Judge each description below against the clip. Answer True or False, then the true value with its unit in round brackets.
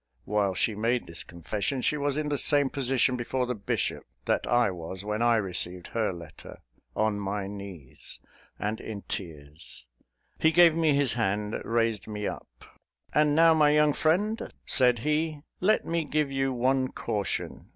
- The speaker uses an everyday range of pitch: False (6.4 semitones)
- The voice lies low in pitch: True (120 Hz)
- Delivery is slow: False (165 wpm)